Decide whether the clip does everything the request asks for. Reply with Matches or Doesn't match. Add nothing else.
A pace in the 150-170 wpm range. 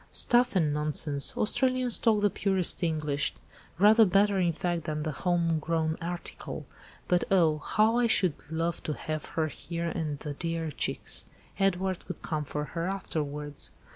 Matches